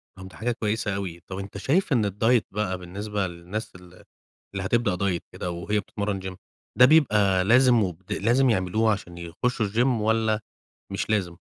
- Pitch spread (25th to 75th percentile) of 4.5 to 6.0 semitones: No, average, 3.3 semitones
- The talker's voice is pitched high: No, low, 105 Hz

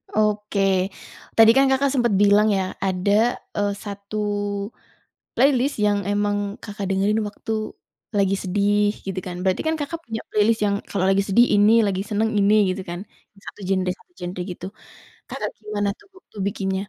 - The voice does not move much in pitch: Yes, narrow, 1.9 semitones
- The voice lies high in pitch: Yes, high, 205 Hz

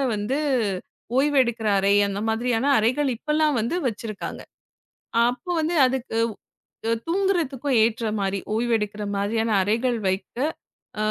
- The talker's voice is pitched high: Yes, high, 235 Hz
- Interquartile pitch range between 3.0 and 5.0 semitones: Yes, average, 4.0 semitones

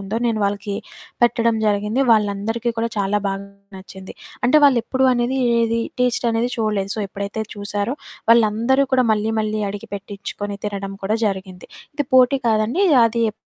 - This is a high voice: Yes, high, 215 Hz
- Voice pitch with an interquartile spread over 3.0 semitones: No, narrow, 2.6 semitones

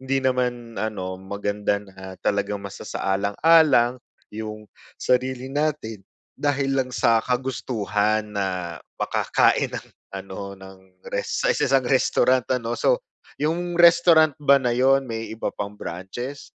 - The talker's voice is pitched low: Yes, low, 115 Hz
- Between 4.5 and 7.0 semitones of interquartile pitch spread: Yes, average, 5.0 semitones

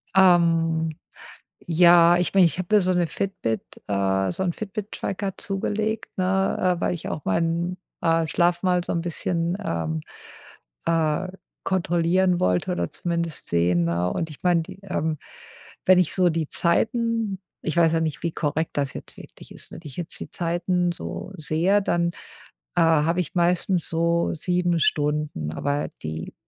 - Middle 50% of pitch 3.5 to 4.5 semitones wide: No, narrow, 2.6 semitones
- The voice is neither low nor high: Yes, medium, 170 Hz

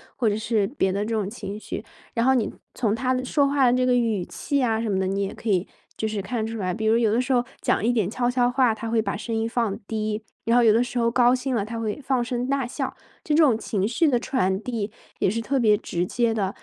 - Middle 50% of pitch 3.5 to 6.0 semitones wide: No, average, 2.7 semitones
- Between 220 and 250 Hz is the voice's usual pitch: Yes, high, 230 Hz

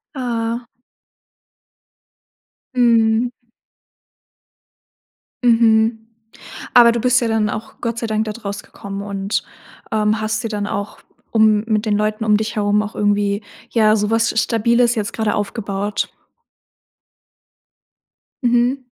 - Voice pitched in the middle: No, high, 220 Hz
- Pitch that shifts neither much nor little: No, narrow, 1.8 semitones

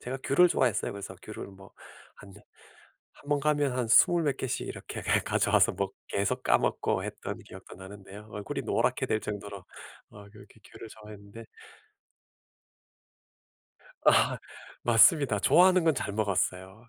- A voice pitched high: No, low, 105 Hz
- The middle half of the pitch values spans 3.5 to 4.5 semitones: No, average, 5.0 semitones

